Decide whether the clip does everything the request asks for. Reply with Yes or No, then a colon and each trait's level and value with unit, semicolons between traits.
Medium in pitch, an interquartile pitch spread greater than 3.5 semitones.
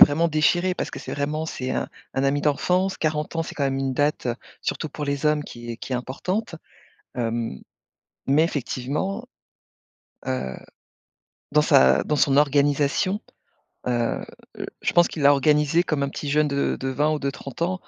No: medium, 145 Hz; narrow, 2.6 semitones